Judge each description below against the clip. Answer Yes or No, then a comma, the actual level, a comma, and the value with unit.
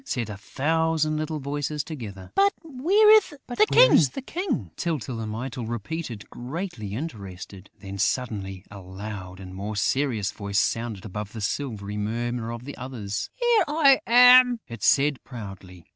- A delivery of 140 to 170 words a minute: Yes, average, 145 wpm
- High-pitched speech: No, low, 120 Hz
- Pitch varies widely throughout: Yes, wide, 7.9 semitones